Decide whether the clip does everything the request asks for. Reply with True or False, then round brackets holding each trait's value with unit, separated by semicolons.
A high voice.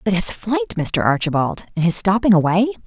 False (180 Hz)